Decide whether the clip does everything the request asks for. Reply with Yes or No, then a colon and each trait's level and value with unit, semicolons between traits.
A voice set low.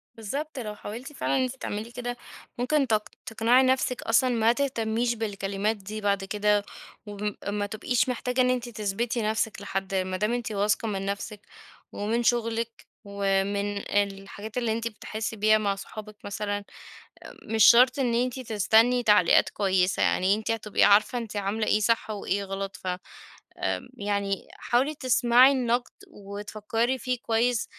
No: high, 220 Hz